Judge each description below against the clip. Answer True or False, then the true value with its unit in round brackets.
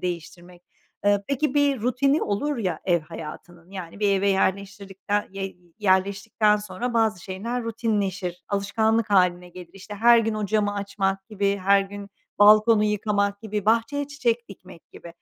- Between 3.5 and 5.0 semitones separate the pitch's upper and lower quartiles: False (2.7 semitones)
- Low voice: False (200 Hz)